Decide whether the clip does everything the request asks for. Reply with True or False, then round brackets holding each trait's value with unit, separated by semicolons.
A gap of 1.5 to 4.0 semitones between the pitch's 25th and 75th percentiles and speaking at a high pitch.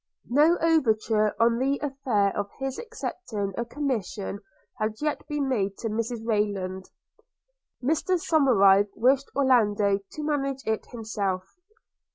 False (5.2 semitones; 235 Hz)